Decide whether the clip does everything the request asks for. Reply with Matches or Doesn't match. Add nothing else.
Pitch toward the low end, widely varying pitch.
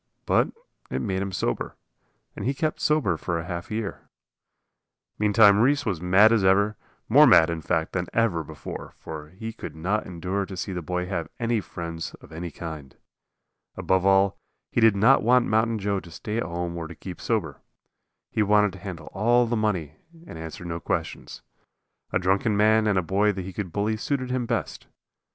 Doesn't match